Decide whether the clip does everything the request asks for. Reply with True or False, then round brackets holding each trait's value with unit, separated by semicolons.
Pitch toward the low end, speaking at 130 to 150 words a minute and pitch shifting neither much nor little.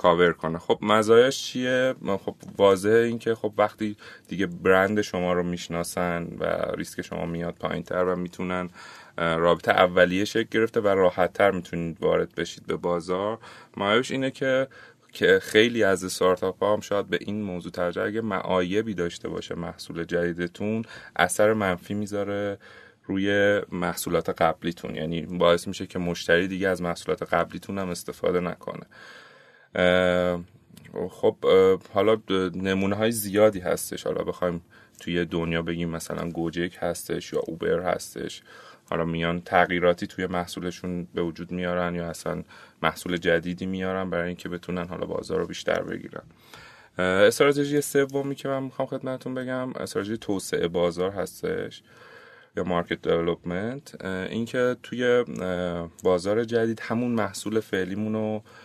True (95 Hz; 135 wpm; 3.8 semitones)